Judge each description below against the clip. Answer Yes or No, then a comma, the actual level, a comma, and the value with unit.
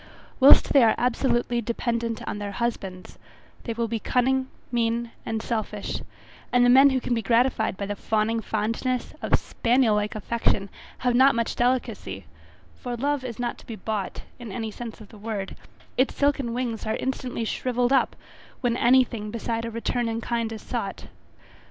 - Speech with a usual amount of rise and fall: No, narrow, 2.1 semitones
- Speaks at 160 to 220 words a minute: Yes, average, 175 wpm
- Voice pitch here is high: Yes, high, 235 Hz